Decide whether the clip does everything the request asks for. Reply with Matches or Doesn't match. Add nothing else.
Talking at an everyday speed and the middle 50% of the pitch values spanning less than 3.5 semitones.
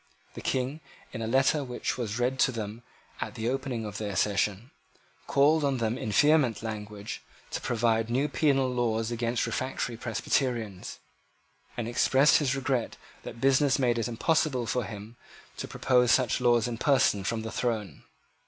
Matches